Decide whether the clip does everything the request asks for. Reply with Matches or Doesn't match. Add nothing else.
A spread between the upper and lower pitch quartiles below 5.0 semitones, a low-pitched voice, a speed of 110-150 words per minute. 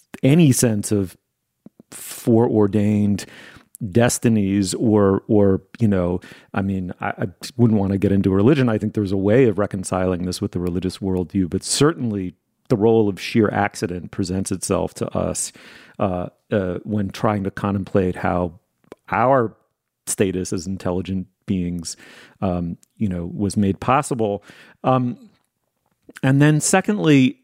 Matches